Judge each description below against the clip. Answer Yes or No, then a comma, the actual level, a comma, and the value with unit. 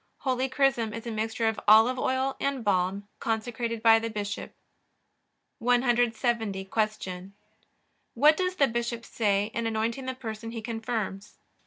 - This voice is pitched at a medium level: No, high, 230 Hz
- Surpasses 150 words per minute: No, average, 140 wpm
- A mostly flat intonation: Yes, narrow, 2.3 semitones